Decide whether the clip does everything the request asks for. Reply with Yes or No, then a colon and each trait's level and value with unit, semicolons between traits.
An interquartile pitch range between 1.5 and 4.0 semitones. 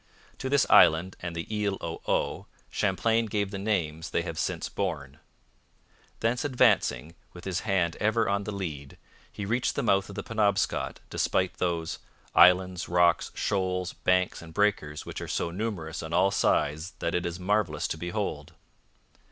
Yes: average, 3.5 semitones